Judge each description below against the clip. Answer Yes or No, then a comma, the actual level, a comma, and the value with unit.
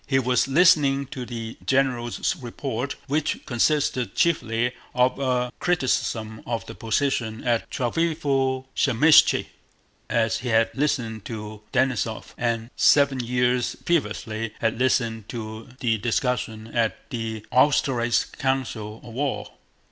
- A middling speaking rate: No, slow, 115 wpm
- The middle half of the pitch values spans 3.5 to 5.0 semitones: No, average, 3.1 semitones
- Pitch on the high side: No, low, 125 Hz